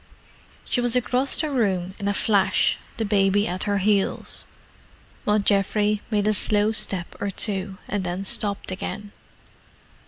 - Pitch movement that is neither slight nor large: No, narrow, 1.6 semitones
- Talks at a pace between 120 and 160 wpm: Yes, average, 150 wpm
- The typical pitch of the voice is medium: No, high, 205 Hz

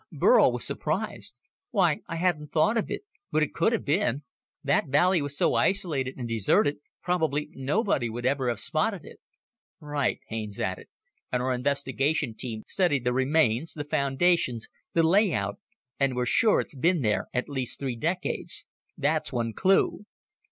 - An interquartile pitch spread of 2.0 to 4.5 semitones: No, average, 5.2 semitones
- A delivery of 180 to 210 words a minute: No, average, 160 wpm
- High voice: No, medium, 145 Hz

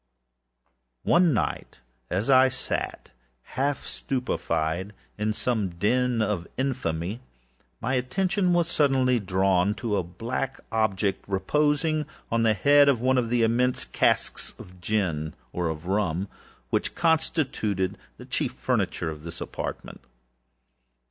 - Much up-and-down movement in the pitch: Yes, wide, 5.9 semitones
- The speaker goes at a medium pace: No, slow, 130 wpm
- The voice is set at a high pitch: No, low, 115 Hz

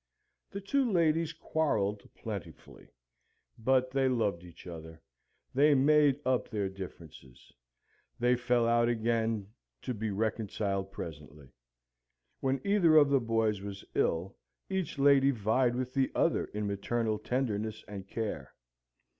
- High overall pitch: No, low, 115 Hz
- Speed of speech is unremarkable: No, slow, 130 wpm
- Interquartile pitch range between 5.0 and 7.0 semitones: Yes, average, 5.3 semitones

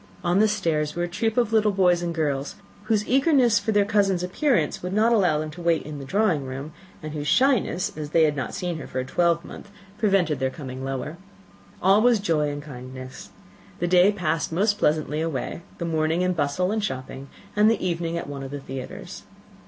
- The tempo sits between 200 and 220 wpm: Yes, fast, 205 wpm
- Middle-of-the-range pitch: Yes, medium, 170 Hz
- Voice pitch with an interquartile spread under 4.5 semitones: No, wide, 5.5 semitones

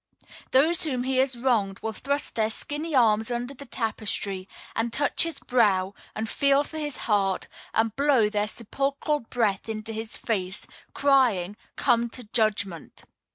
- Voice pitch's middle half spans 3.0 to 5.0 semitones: Yes, average, 4.5 semitones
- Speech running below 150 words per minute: No, average, 155 wpm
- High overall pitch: Yes, high, 230 Hz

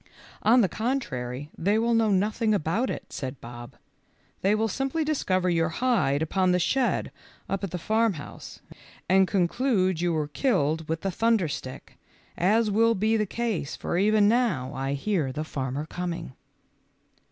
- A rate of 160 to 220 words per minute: Yes, average, 165 wpm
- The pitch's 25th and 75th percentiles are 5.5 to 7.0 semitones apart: Yes, wide, 6.0 semitones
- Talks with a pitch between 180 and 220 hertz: Yes, high, 190 Hz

